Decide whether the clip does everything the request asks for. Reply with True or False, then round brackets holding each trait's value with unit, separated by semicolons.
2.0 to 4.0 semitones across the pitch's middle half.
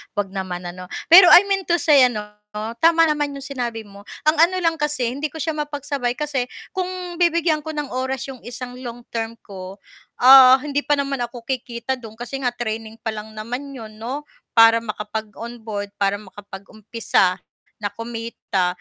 False (4.8 semitones)